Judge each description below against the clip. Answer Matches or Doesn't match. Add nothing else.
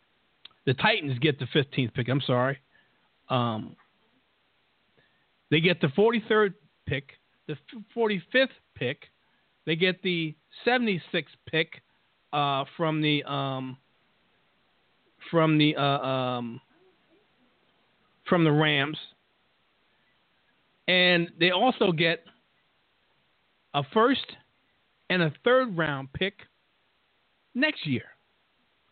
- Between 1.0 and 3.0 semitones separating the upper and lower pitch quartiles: Doesn't match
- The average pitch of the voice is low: Doesn't match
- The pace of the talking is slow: Matches